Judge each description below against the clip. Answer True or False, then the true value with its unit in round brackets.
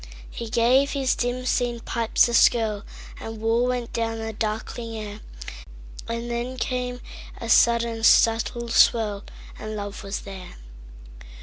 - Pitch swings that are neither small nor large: False (1.9 semitones)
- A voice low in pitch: False (230 Hz)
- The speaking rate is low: True (115 wpm)